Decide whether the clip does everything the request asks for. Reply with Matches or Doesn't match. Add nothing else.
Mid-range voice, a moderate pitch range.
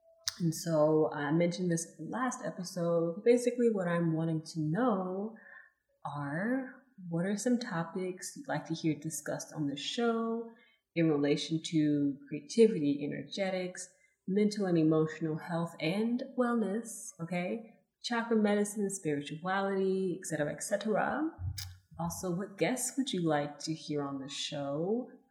Doesn't match